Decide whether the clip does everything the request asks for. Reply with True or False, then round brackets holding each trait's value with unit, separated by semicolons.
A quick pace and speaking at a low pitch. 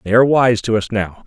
True (285 wpm; 110 Hz)